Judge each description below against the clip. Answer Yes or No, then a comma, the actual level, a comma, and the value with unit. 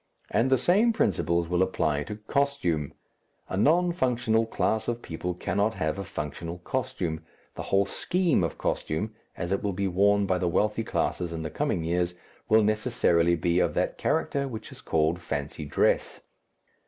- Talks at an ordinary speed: Yes, average, 170 wpm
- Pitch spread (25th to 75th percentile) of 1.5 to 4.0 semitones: No, average, 5.1 semitones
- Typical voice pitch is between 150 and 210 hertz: No, very low, 95 Hz